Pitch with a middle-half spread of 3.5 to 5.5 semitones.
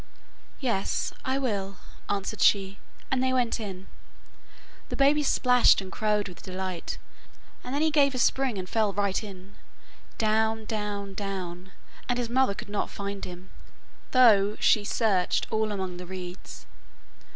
Yes: average, 4.0 semitones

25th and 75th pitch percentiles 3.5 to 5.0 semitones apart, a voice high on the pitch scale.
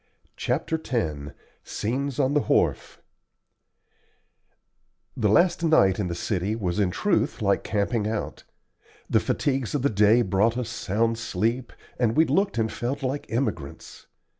No: average, 4.7 semitones; low, 115 Hz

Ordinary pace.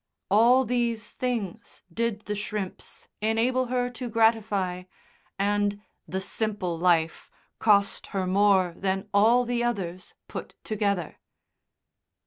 No: slow, 115 wpm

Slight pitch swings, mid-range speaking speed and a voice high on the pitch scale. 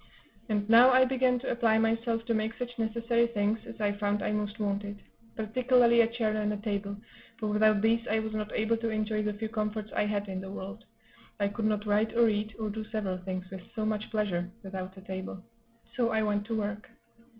No: narrow, 1.8 semitones; fast, 215 wpm; high, 215 Hz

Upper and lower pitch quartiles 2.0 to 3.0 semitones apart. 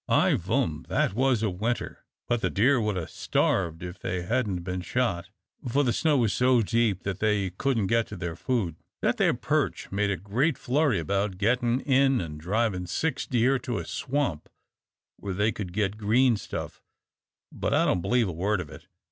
No: average, 5.2 semitones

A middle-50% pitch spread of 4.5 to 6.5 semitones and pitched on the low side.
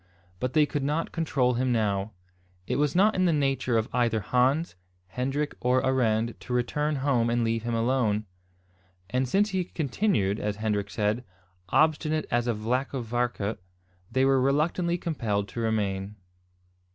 Yes: average, 4.8 semitones; low, 125 Hz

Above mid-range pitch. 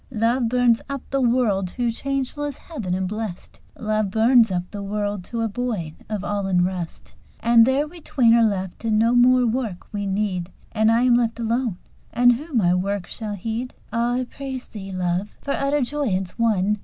Yes: high, 225 Hz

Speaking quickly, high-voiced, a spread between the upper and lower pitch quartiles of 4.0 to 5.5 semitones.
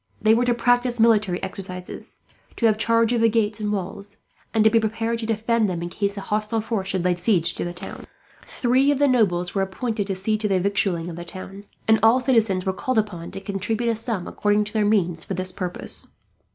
No: fast, 230 wpm; high, 210 Hz; average, 3.2 semitones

